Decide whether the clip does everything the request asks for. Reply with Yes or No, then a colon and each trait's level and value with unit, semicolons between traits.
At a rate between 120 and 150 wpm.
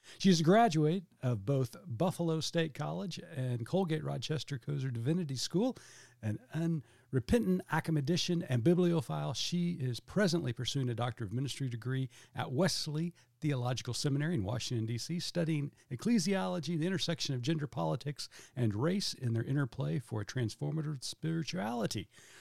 Yes: average, 140 wpm